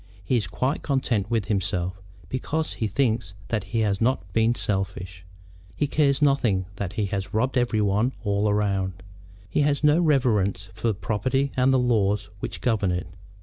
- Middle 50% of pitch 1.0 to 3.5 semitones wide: No, average, 4.8 semitones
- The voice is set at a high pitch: No, low, 105 Hz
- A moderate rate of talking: Yes, average, 170 wpm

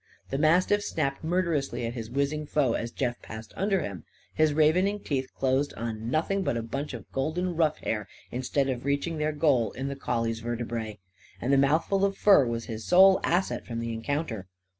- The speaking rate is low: No, average, 190 wpm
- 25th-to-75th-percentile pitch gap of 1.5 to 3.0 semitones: No, average, 5.3 semitones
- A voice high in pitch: No, medium, 140 Hz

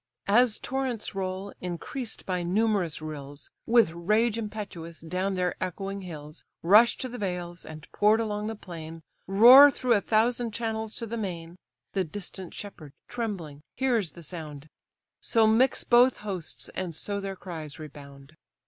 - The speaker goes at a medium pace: Yes, average, 150 wpm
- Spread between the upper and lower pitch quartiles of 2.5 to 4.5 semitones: No, average, 5.1 semitones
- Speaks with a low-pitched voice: No, high, 195 Hz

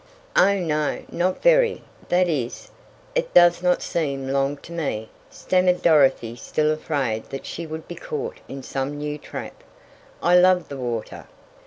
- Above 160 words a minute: No, average, 155 wpm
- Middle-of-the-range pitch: Yes, medium, 155 Hz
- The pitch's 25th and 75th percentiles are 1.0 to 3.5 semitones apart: No, average, 4.7 semitones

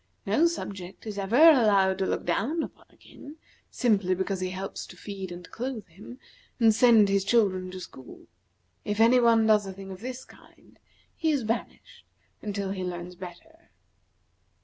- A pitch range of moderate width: Yes, average, 4.1 semitones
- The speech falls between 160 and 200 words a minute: Yes, average, 170 wpm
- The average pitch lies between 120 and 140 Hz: No, high, 205 Hz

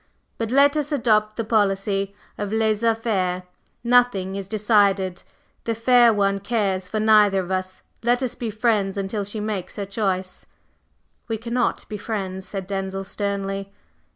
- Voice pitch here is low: No, high, 205 Hz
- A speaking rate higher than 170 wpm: No, average, 155 wpm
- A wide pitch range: No, narrow, 2.6 semitones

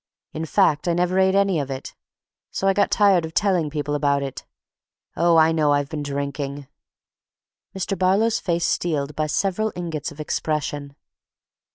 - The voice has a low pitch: No, medium, 160 Hz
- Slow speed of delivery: No, average, 160 wpm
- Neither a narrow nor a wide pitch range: Yes, average, 4.1 semitones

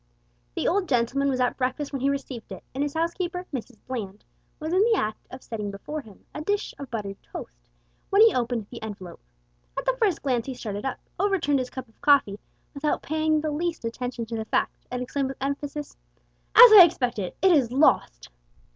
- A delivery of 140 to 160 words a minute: No, average, 200 wpm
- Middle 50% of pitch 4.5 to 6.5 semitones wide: Yes, average, 5.2 semitones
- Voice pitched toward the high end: Yes, very high, 270 Hz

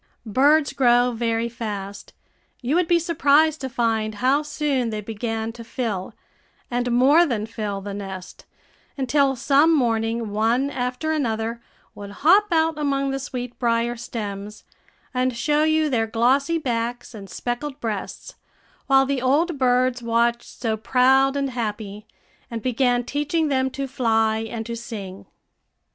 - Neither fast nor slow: Yes, average, 145 wpm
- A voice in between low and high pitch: No, high, 245 Hz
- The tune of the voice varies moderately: Yes, average, 3.7 semitones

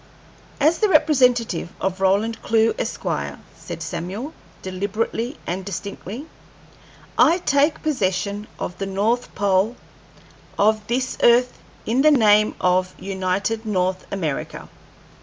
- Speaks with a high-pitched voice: Yes, high, 210 Hz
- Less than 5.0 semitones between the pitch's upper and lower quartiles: Yes, average, 4.6 semitones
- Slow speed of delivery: Yes, slow, 115 wpm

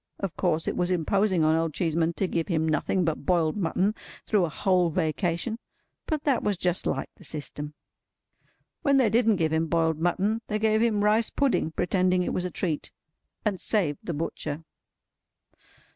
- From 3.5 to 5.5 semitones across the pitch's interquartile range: Yes, average, 4.4 semitones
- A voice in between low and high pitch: Yes, medium, 180 Hz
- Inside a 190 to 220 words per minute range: No, average, 175 wpm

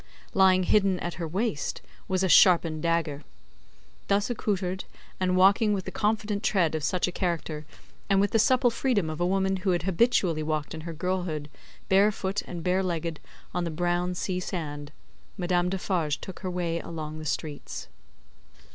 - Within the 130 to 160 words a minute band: No, average, 175 wpm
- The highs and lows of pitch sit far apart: No, average, 2.7 semitones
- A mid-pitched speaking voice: Yes, medium, 180 Hz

